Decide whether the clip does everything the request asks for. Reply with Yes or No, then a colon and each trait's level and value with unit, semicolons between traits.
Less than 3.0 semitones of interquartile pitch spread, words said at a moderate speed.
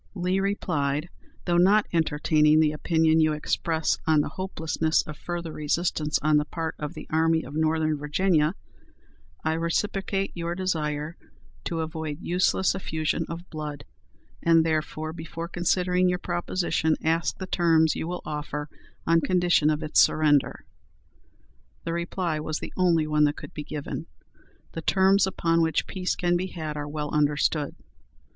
Yes: narrow, 2.4 semitones; average, 150 wpm